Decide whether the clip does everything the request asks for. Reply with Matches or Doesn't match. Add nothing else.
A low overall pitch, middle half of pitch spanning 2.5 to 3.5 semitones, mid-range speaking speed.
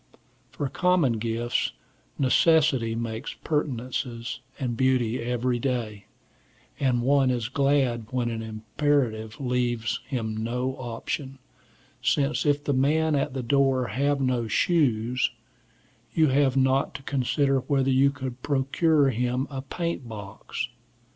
Doesn't match